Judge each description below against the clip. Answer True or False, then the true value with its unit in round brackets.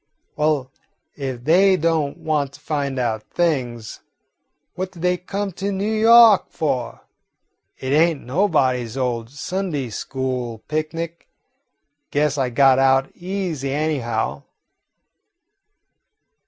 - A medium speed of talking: False (110 wpm)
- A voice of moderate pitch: True (145 Hz)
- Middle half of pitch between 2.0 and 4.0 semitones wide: False (5.1 semitones)